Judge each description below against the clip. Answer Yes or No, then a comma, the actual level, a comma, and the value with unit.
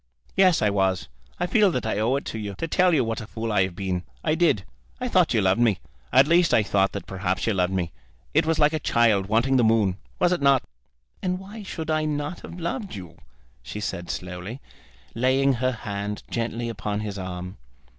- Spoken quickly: Yes, fast, 215 wpm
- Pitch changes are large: Yes, wide, 7.8 semitones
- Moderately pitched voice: No, low, 115 Hz